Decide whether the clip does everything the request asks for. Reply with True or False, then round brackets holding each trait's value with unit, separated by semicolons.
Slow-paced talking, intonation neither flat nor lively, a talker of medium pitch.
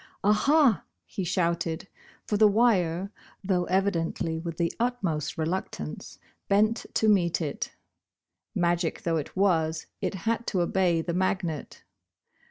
True (130 wpm; 3.5 semitones; 180 Hz)